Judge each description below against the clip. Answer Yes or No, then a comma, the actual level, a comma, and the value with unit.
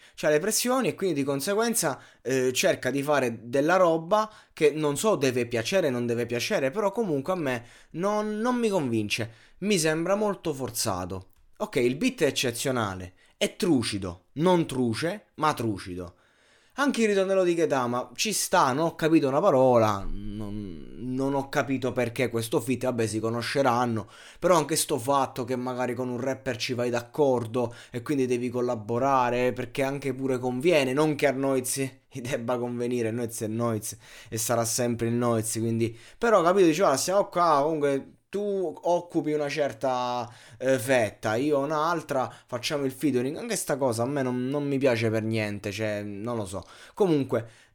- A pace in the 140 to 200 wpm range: Yes, fast, 170 wpm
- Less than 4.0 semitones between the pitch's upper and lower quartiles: No, average, 4.5 semitones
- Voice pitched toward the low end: Yes, low, 130 Hz